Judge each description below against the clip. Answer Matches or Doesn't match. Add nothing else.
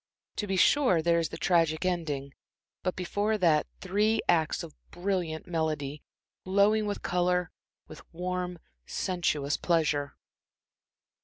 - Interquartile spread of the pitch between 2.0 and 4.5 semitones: Matches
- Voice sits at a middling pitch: Matches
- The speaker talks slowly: Matches